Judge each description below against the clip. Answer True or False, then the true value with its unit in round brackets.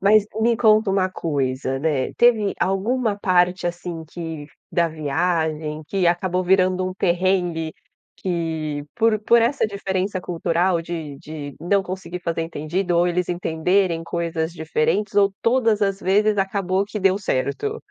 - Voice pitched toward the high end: False (180 Hz)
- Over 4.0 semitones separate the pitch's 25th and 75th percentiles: False (3.3 semitones)